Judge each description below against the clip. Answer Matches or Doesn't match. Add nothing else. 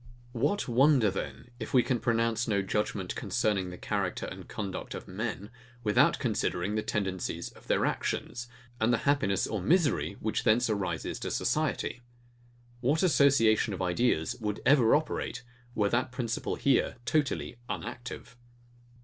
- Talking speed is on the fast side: Doesn't match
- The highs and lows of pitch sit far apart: Doesn't match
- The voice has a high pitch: Doesn't match